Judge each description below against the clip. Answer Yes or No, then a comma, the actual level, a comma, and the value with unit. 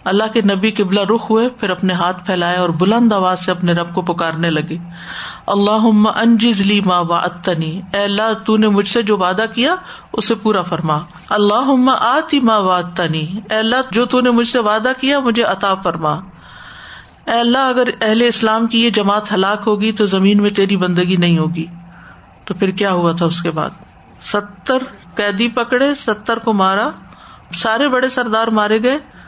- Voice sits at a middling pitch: No, high, 205 Hz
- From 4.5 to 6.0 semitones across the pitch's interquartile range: No, average, 4.0 semitones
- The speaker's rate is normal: Yes, average, 180 wpm